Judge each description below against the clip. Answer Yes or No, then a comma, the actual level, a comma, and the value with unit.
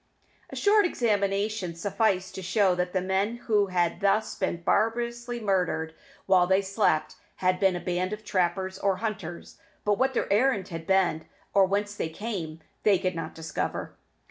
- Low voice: No, high, 190 Hz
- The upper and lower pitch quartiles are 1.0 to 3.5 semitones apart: Yes, average, 2.9 semitones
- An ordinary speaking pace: Yes, average, 170 wpm